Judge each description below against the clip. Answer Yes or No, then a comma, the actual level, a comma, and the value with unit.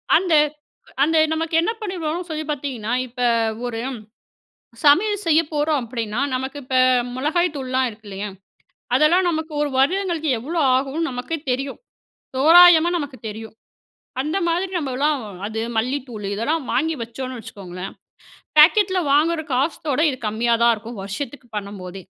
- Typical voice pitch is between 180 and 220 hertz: No, very high, 280 Hz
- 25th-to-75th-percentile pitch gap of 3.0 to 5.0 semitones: No, wide, 5.5 semitones